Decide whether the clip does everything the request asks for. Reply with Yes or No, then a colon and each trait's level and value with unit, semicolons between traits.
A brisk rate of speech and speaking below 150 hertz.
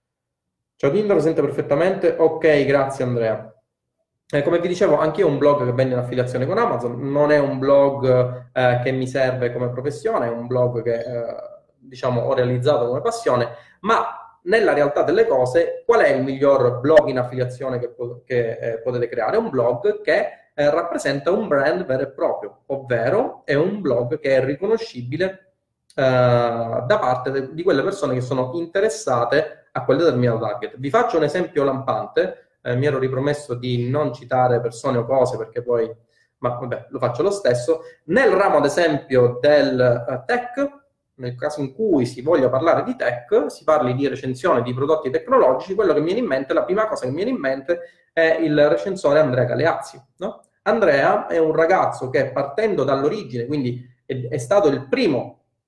Yes: fast, 185 wpm; low, 135 Hz